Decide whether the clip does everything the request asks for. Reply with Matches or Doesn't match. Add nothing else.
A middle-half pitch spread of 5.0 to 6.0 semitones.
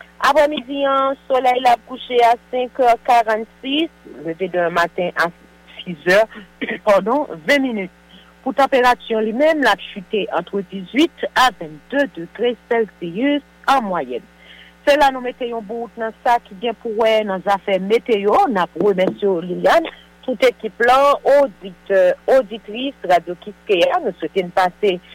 Matches